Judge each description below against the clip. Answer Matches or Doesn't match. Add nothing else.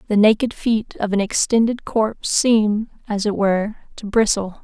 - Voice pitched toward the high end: Matches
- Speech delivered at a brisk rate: Doesn't match